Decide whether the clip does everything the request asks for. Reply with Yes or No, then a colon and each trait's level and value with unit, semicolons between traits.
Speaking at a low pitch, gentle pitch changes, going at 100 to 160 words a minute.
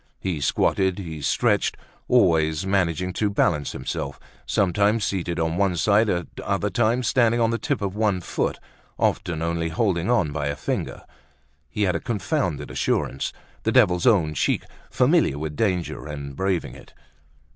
No: very low, 90 Hz; average, 4.2 semitones; average, 155 wpm